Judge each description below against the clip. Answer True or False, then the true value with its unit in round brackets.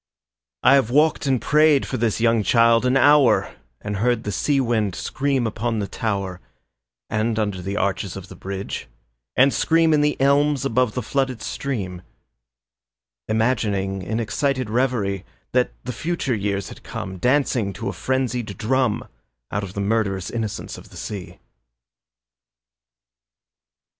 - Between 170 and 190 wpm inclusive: False (150 wpm)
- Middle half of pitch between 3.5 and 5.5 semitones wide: True (4.7 semitones)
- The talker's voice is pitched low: True (115 Hz)